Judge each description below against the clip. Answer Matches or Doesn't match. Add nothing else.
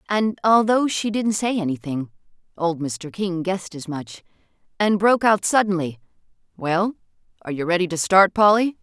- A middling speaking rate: Matches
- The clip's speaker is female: Matches